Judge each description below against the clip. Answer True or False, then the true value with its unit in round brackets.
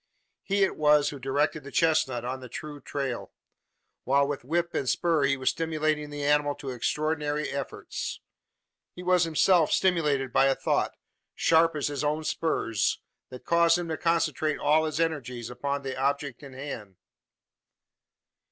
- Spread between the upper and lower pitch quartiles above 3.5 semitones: False (2.9 semitones)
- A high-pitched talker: False (145 Hz)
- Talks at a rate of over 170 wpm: False (160 wpm)